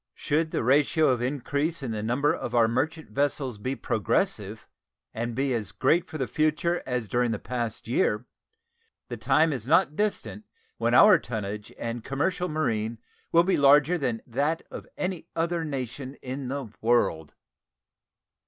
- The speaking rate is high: No, average, 160 wpm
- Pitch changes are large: No, average, 5.0 semitones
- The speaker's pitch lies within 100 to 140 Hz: Yes, low, 135 Hz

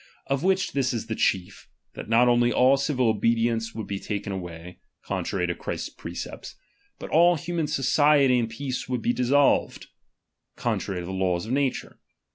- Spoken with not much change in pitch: No, average, 5.1 semitones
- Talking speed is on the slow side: No, average, 170 wpm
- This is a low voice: Yes, low, 120 Hz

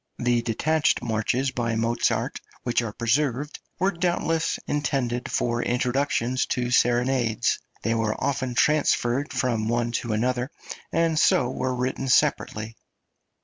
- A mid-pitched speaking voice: No, low, 125 Hz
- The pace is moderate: No, slow, 125 wpm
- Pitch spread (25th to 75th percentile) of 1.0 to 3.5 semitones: Yes, average, 2.8 semitones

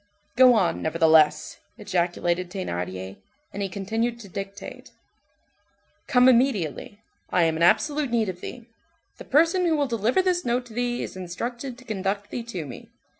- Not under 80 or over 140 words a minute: No, average, 160 wpm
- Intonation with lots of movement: Yes, wide, 5.9 semitones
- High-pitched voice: Yes, high, 210 Hz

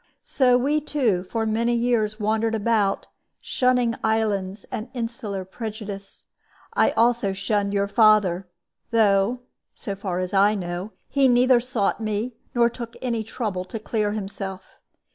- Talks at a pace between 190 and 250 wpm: No, average, 140 wpm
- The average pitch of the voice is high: Yes, high, 220 Hz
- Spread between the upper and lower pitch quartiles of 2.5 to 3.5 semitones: Yes, average, 3.0 semitones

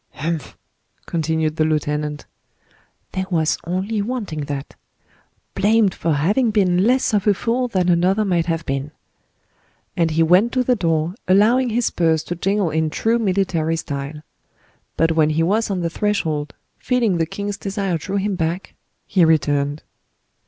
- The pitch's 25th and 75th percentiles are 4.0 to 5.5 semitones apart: Yes, average, 4.5 semitones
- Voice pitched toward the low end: No, medium, 175 Hz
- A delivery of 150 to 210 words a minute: Yes, average, 155 wpm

